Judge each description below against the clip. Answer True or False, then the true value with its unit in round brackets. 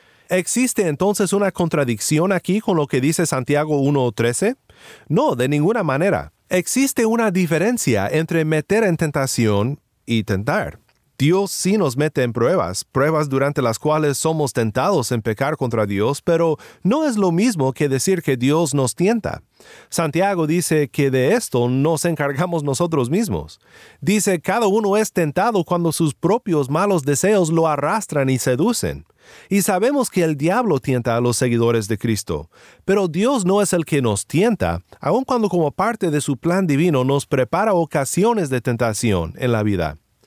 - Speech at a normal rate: True (160 wpm)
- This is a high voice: False (155 Hz)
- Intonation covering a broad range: True (6.3 semitones)